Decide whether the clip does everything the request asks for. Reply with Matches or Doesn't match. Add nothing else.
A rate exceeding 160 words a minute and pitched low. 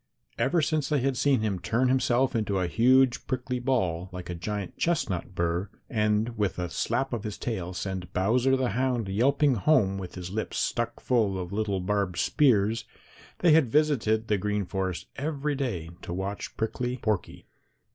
Matches